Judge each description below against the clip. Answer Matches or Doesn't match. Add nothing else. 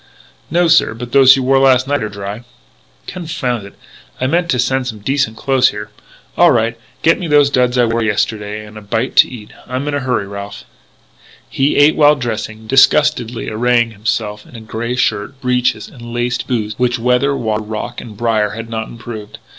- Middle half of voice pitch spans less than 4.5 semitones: Matches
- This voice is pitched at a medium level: Doesn't match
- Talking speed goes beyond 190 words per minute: Matches